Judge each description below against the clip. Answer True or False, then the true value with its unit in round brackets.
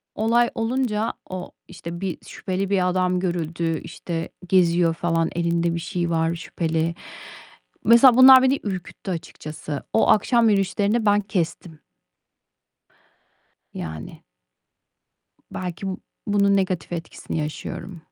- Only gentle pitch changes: False (3.4 semitones)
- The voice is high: False (180 Hz)